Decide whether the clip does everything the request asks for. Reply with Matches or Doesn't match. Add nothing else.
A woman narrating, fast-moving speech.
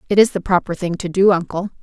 Matches